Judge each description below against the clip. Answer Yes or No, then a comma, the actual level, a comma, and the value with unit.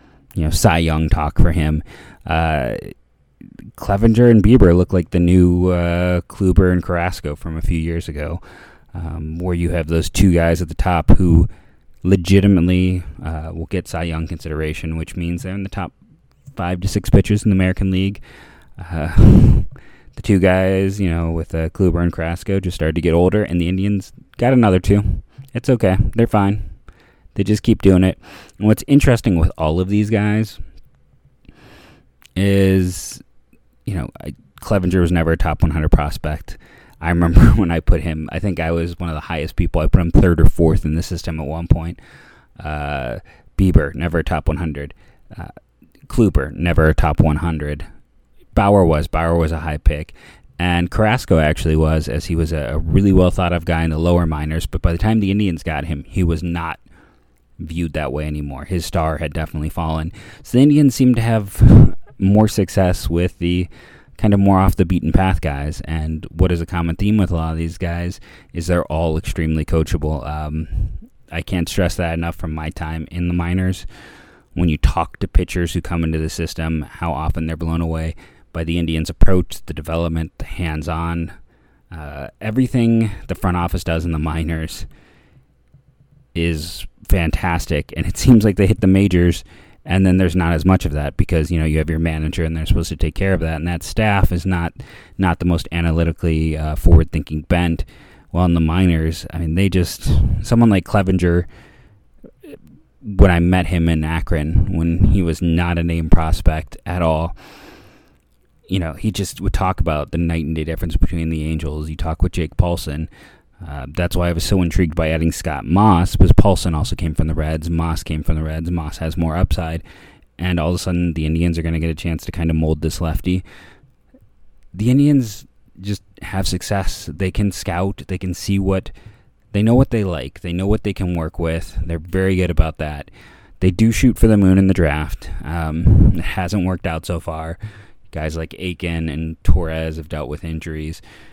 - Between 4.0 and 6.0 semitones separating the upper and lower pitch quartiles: No, average, 2.9 semitones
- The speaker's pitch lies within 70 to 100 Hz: Yes, very low, 85 Hz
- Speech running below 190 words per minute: No, average, 195 wpm